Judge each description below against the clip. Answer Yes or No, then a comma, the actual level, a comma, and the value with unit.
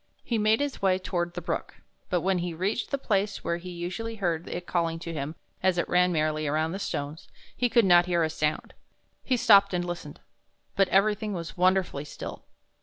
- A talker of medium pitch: Yes, medium, 180 Hz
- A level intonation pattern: No, average, 3.0 semitones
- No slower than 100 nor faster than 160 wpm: No, average, 200 wpm